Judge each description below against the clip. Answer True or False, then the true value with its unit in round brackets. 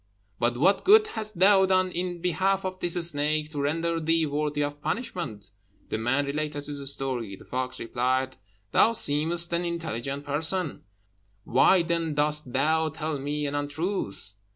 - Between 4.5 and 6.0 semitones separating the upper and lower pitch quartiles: False (3.5 semitones)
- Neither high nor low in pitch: True (150 Hz)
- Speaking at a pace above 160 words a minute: False (155 wpm)